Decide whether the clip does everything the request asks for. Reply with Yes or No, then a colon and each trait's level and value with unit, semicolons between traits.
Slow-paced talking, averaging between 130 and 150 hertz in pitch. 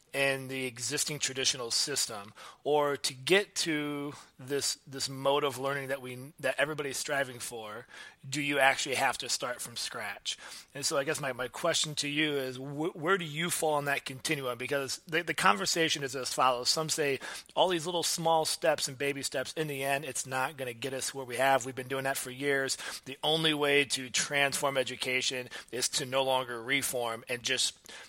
No: average, 200 wpm; medium, 140 Hz